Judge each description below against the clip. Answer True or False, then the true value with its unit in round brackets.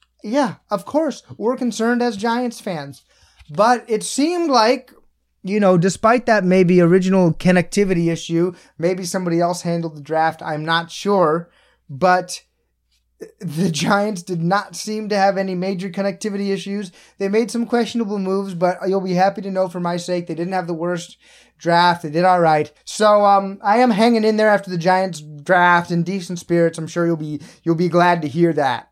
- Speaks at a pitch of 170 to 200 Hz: True (185 Hz)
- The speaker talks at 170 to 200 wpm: True (185 wpm)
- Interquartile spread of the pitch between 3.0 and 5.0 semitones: True (3.3 semitones)